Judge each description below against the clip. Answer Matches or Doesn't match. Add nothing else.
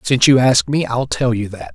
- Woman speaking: Doesn't match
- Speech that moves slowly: Doesn't match